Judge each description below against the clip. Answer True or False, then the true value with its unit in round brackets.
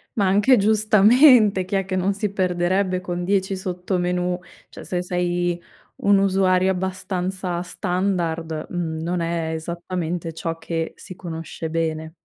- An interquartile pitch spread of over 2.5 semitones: False (2.0 semitones)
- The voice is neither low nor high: True (180 Hz)